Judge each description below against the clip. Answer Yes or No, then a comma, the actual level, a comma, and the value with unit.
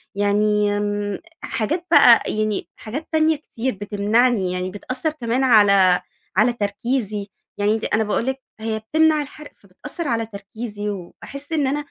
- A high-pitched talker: Yes, high, 220 Hz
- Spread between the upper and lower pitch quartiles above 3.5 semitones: Yes, average, 4.5 semitones